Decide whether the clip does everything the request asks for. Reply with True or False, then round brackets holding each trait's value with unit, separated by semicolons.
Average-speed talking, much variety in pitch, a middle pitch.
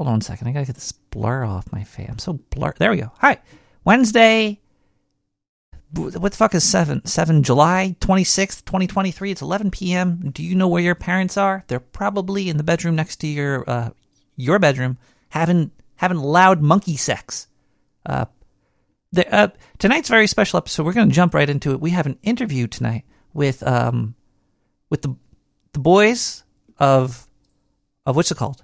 True (185 wpm; 6.7 semitones; 160 Hz)